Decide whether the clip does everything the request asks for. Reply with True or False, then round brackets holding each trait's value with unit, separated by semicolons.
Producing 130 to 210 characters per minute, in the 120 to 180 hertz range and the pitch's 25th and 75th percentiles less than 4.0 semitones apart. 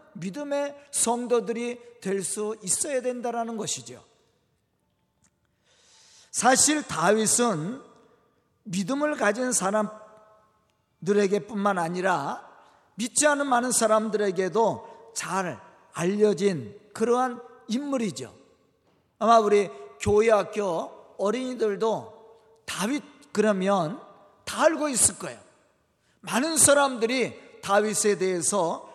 False (205 characters per minute; 220 Hz; 3.3 semitones)